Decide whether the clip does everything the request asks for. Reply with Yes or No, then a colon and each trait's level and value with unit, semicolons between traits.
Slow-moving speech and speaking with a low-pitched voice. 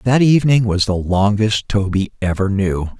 No: average, 160 wpm; low, 105 Hz